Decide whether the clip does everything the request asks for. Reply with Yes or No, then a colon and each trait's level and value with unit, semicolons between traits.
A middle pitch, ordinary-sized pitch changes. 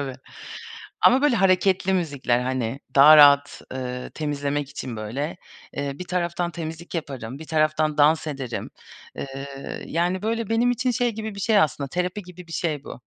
Yes: medium, 155 Hz; average, 4.8 semitones